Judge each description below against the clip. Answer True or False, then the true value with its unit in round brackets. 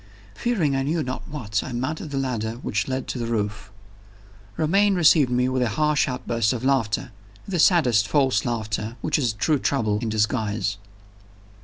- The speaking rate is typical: True (170 wpm)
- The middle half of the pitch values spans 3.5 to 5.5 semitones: True (4.9 semitones)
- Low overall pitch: True (125 Hz)